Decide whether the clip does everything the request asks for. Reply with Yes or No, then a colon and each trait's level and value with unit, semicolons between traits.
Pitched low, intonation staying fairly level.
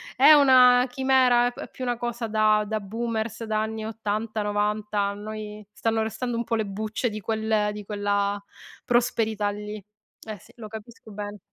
No: high, 220 Hz; narrow, 2.0 semitones